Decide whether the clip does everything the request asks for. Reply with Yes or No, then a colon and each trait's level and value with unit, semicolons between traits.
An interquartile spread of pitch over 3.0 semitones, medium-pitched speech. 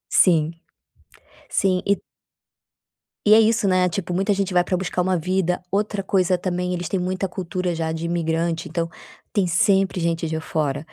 No: narrow, 2.4 semitones; medium, 180 Hz